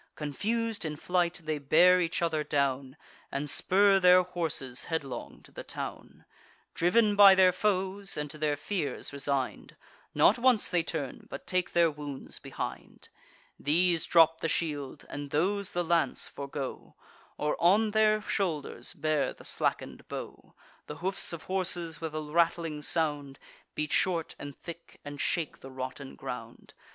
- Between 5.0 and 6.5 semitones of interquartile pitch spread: No, average, 3.9 semitones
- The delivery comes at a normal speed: Yes, average, 150 wpm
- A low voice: No, medium, 165 Hz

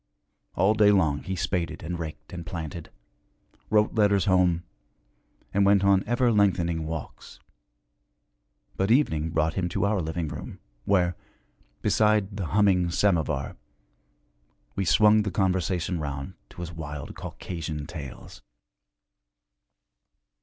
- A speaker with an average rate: No, slow, 120 wpm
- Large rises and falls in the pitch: No, average, 3.7 semitones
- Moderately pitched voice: No, very low, 90 Hz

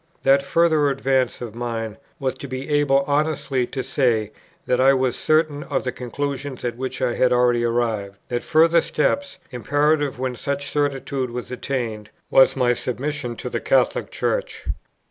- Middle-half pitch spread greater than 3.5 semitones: No, average, 2.8 semitones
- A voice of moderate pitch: No, low, 130 Hz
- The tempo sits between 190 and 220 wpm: No, average, 165 wpm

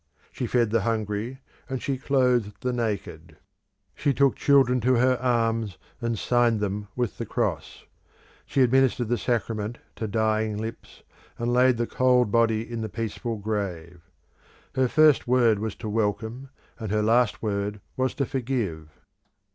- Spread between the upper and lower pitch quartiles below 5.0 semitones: Yes, average, 2.9 semitones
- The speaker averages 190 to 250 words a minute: No, average, 150 wpm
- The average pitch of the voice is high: No, low, 115 Hz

